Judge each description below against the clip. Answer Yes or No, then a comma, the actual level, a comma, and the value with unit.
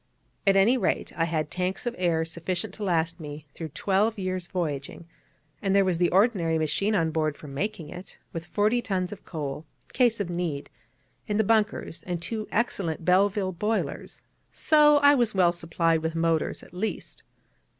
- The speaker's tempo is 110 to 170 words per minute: No, average, 180 wpm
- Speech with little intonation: No, average, 4.2 semitones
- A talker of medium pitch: Yes, medium, 180 Hz